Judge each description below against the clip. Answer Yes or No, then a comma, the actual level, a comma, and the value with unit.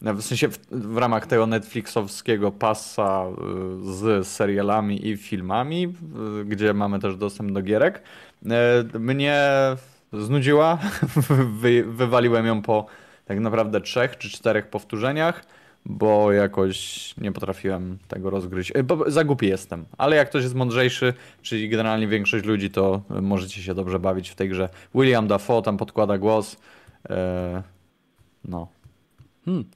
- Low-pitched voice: Yes, low, 110 Hz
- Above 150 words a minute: No, average, 140 wpm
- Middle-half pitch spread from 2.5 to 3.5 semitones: No, average, 4.0 semitones